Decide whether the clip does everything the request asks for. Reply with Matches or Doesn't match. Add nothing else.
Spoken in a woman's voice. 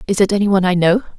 Matches